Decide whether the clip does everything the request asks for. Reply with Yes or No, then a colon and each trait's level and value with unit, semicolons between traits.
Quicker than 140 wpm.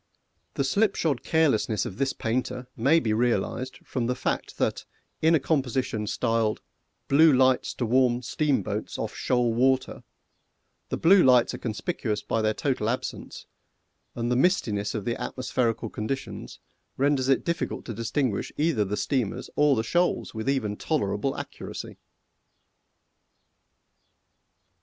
No: slow, 135 wpm